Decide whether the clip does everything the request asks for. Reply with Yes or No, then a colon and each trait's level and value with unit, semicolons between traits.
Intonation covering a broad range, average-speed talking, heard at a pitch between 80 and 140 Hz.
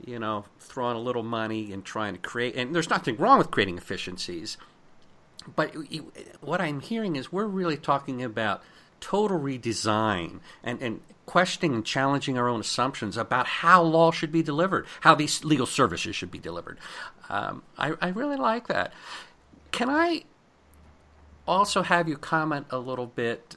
Yes: wide, 6.8 semitones; average, 165 wpm; low, 135 Hz